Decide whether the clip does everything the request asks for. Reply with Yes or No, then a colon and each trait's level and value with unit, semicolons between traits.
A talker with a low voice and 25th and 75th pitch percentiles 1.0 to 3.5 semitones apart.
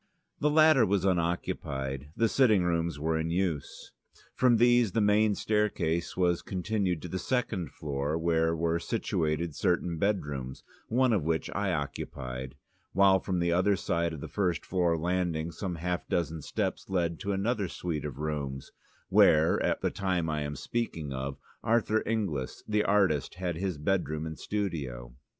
No: very low, 85 Hz; average, 4.4 semitones